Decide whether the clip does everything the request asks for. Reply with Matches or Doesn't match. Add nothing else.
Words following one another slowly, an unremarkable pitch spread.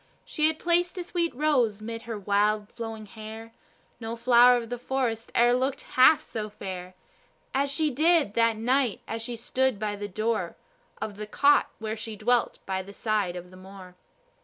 Doesn't match